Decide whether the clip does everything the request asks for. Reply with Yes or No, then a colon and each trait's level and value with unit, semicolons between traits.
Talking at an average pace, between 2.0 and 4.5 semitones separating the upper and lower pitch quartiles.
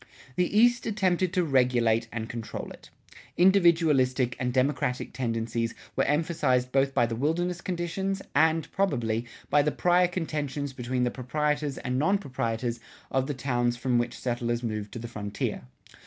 No: average, 155 wpm; wide, 5.5 semitones